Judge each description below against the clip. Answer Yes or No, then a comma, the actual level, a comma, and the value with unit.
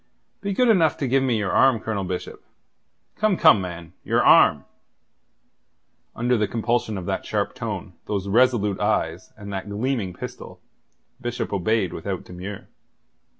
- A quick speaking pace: No, average, 150 wpm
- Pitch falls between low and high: No, low, 110 Hz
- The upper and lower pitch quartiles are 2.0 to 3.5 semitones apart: No, average, 4.9 semitones